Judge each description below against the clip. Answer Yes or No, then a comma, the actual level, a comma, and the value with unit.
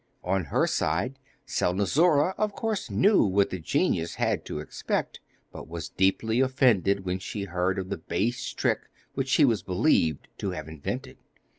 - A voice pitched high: No, low, 100 Hz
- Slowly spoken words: No, average, 160 wpm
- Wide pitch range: Yes, wide, 6.5 semitones